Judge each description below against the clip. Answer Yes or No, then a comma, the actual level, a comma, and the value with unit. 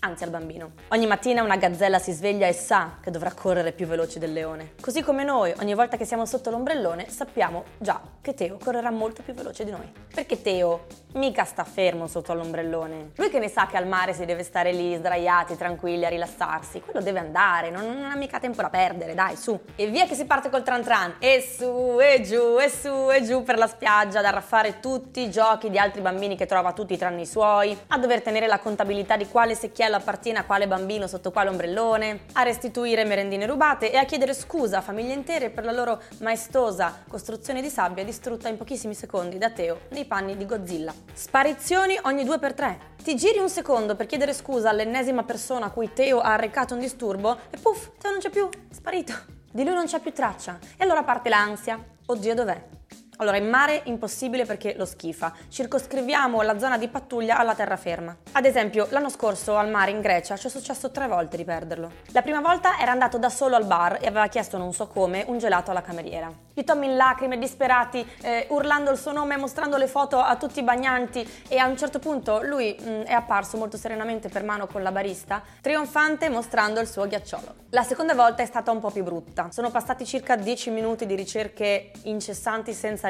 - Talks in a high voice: Yes, high, 225 Hz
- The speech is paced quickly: Yes, fast, 210 wpm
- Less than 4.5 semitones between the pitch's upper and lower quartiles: No, average, 4.8 semitones